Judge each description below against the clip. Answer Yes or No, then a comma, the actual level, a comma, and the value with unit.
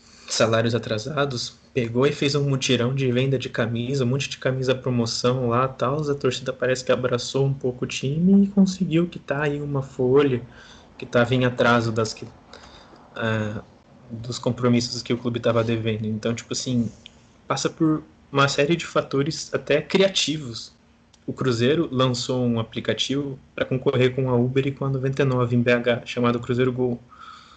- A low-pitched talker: Yes, low, 125 Hz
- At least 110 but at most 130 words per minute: No, average, 170 wpm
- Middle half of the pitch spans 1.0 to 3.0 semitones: Yes, narrow, 2.4 semitones